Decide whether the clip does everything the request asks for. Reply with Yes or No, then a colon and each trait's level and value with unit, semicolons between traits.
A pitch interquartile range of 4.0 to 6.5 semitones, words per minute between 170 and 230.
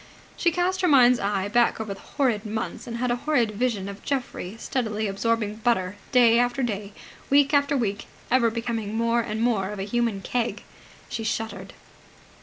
No: average, 2.9 semitones; average, 180 wpm